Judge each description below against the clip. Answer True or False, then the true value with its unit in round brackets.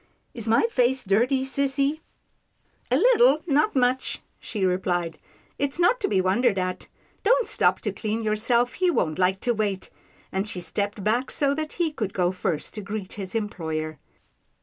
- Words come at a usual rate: True (180 wpm)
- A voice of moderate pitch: False (220 Hz)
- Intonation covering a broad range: True (6.5 semitones)